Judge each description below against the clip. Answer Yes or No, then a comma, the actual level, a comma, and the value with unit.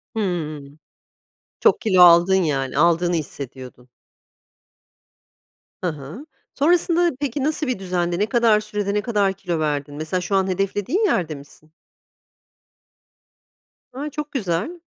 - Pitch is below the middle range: No, high, 190 Hz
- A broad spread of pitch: Yes, wide, 6.7 semitones